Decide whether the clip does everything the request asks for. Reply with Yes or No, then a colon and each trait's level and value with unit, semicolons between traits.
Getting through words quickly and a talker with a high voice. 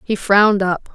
No: average, 190 wpm; high, 195 Hz